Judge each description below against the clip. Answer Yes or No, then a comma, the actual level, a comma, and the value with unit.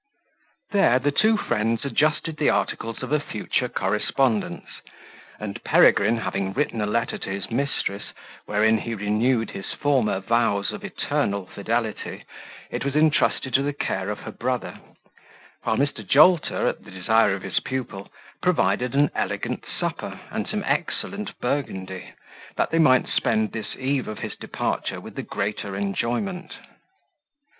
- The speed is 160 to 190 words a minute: No, average, 150 wpm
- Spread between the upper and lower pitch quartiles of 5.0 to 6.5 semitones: Yes, average, 5.3 semitones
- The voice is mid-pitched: No, low, 115 Hz